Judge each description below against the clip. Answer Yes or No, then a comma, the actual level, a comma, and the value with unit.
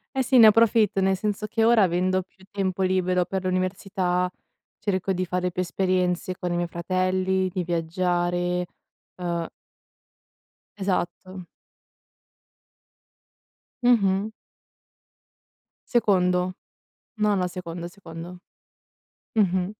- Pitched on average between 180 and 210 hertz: Yes, medium, 185 Hz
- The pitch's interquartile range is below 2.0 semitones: Yes, narrow, 1.6 semitones